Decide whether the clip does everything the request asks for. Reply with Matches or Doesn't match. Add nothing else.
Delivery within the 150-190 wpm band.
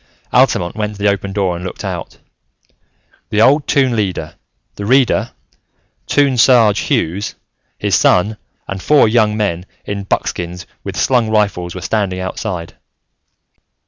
Doesn't match